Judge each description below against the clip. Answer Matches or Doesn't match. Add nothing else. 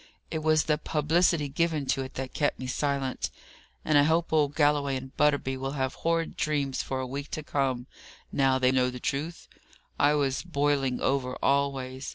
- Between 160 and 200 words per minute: Matches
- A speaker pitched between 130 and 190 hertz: Matches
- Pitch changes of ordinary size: Doesn't match